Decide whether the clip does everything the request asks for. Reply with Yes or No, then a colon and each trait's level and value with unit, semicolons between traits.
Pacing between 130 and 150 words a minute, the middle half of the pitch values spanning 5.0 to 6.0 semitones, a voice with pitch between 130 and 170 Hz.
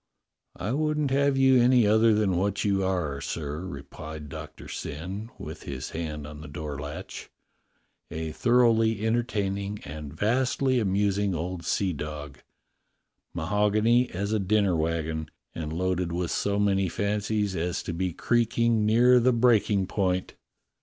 No: average, 145 wpm; wide, 5.4 semitones; low, 100 Hz